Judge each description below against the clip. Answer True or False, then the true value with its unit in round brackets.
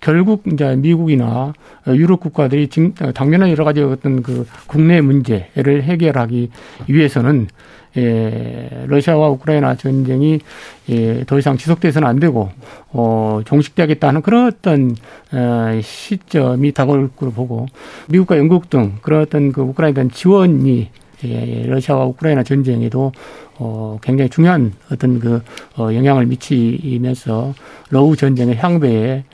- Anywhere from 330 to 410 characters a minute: False (285 characters per minute)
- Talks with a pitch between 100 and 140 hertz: True (135 Hz)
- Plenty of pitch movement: False (3.9 semitones)